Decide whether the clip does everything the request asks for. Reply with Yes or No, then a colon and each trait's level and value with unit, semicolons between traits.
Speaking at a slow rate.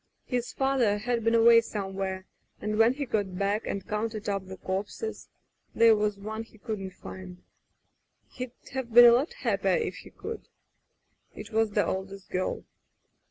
No: average, 165 wpm